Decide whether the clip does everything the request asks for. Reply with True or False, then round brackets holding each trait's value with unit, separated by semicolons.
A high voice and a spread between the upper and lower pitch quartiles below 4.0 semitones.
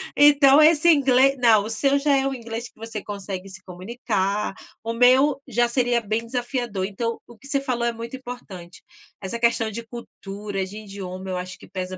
False (230 Hz; 4.4 semitones)